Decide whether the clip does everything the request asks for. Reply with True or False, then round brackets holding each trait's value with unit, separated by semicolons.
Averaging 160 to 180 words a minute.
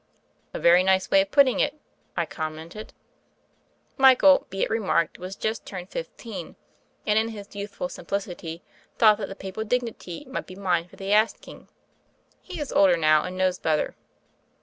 True (170 wpm)